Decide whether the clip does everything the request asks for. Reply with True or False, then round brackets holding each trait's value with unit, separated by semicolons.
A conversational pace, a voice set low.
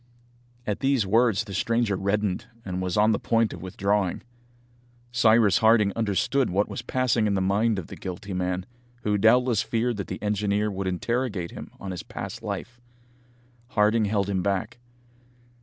True (165 wpm; 105 Hz)